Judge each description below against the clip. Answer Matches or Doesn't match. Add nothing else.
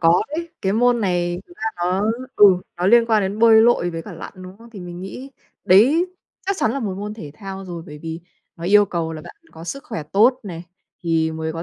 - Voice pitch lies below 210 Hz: Matches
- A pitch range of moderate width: Matches